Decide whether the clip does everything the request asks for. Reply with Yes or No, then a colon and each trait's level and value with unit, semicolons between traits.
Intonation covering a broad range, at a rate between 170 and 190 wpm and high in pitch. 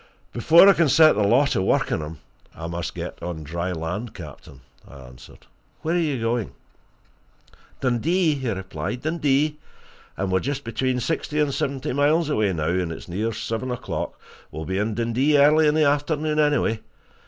No: wide, 8.2 semitones; average, 175 wpm; low, 120 Hz